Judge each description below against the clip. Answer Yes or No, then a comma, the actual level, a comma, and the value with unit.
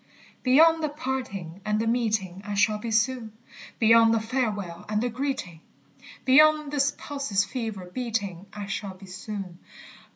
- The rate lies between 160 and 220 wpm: No, average, 150 wpm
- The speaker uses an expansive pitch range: No, average, 4.7 semitones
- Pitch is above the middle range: Yes, high, 220 Hz